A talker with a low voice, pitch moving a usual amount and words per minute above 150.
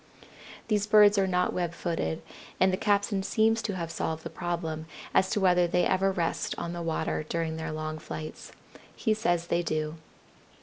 No: medium, 175 Hz; average, 3.4 semitones; average, 180 wpm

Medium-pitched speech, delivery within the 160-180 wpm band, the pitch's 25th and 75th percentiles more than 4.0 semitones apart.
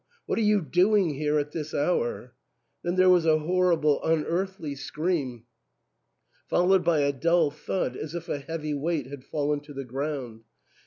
No: medium, 155 Hz; average, 170 wpm; average, 3.6 semitones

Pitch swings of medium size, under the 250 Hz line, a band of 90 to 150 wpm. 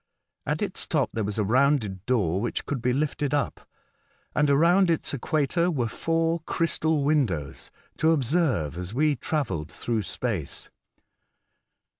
No: wide, 6.5 semitones; medium, 140 Hz; average, 140 wpm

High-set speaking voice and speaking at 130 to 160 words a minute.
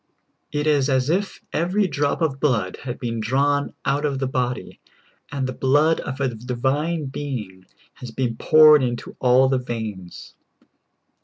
No: low, 135 Hz; average, 155 wpm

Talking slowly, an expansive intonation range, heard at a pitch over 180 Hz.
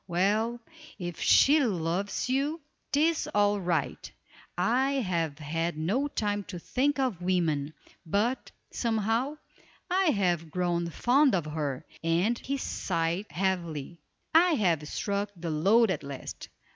Yes: slow, 130 wpm; wide, 6.3 semitones; high, 190 Hz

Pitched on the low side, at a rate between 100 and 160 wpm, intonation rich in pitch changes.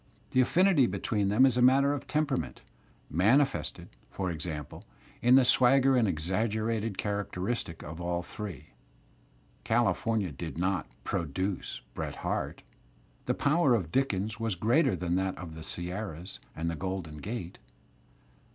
Yes: low, 100 Hz; average, 140 wpm; wide, 5.8 semitones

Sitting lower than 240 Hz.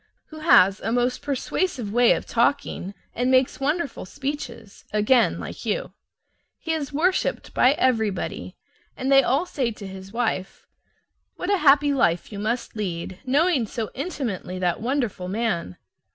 No: high, 245 Hz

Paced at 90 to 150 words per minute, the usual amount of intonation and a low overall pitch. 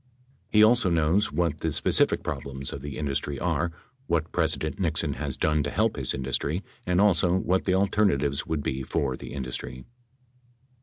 No: average, 165 wpm; average, 4.9 semitones; very low, 80 Hz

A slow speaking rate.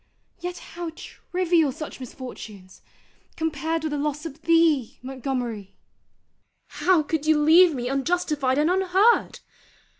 Yes: slow, 120 wpm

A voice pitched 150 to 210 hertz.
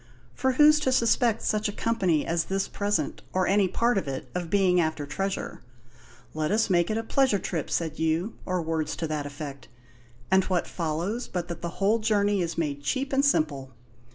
Yes: medium, 185 Hz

